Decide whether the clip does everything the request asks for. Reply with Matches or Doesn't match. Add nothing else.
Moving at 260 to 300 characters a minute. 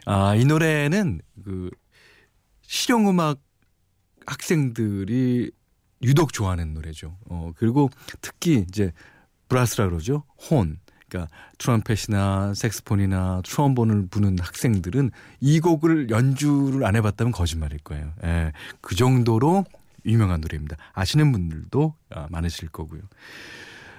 Matches